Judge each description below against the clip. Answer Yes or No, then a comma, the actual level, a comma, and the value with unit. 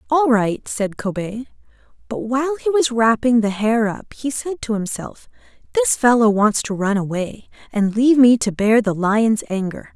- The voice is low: No, high, 230 Hz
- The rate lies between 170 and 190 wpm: Yes, average, 180 wpm